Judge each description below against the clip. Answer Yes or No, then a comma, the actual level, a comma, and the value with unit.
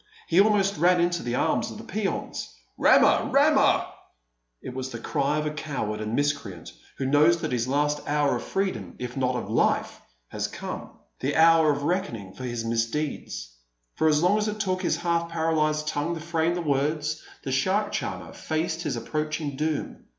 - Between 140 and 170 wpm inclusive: No, average, 185 wpm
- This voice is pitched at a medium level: Yes, medium, 150 Hz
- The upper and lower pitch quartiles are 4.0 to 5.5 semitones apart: Yes, average, 4.4 semitones